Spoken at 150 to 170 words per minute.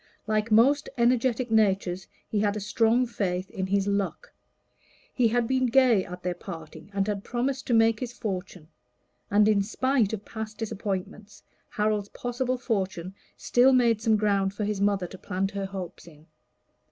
Yes: average, 165 wpm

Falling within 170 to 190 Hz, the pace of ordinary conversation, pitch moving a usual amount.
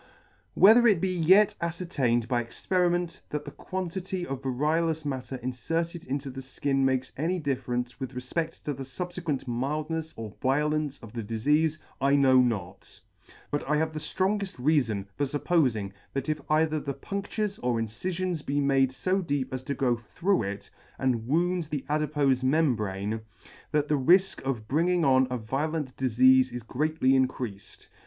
No: medium, 140 Hz; average, 165 wpm; average, 4.3 semitones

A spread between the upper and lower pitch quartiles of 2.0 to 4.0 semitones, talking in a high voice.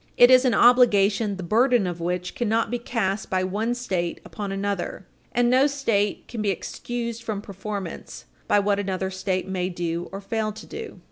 Yes: average, 3.7 semitones; high, 205 Hz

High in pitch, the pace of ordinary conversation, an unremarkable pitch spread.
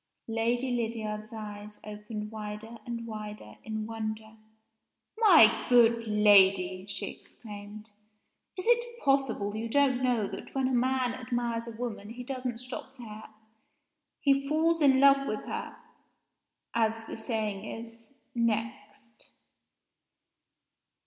No: high, 230 Hz; slow, 120 wpm; average, 3.0 semitones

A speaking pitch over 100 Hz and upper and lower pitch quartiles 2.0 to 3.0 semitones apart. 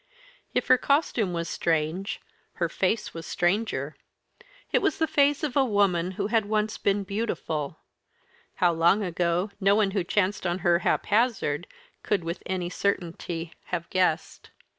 No: high, 190 Hz; average, 3.9 semitones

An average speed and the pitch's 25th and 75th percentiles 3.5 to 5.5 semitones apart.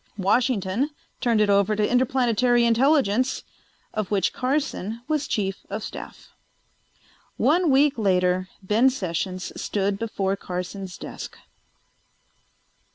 No: slow, 105 wpm; average, 4.8 semitones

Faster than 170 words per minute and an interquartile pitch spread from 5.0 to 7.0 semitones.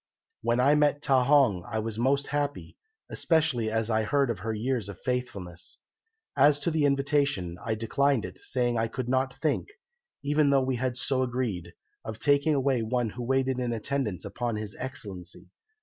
No: average, 180 wpm; average, 3.9 semitones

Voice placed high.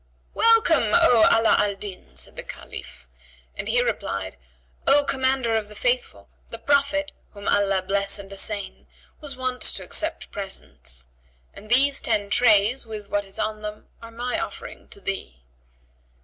Yes: high, 220 Hz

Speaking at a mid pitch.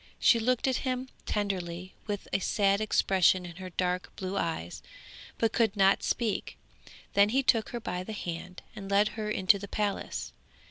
No: high, 200 Hz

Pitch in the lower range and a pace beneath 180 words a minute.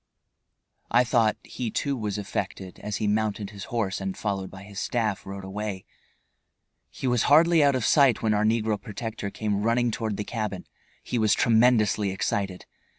Yes: low, 105 Hz; average, 170 wpm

